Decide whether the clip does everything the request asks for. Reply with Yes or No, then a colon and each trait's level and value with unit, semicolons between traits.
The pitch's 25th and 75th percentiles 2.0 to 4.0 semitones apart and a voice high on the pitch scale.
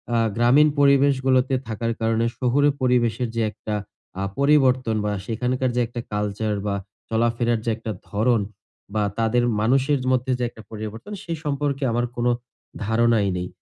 No: average, 2.8 semitones; low, 120 Hz